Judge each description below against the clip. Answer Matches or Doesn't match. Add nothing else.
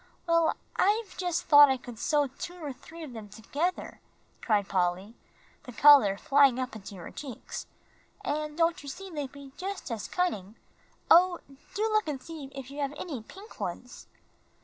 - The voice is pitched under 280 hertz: Doesn't match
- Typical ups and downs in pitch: Doesn't match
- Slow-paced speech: Doesn't match